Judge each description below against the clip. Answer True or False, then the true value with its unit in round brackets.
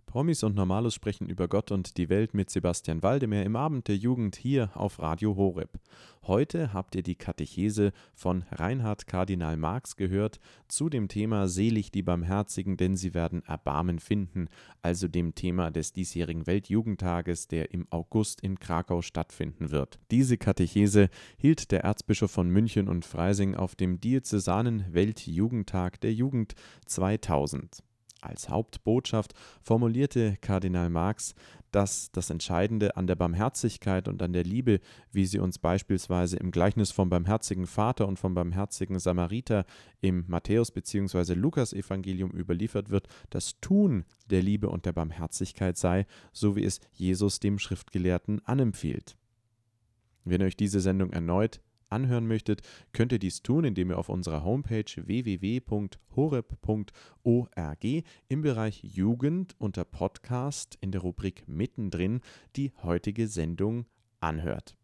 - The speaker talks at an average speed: True (140 wpm)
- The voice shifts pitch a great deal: False (3.6 semitones)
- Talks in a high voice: False (100 Hz)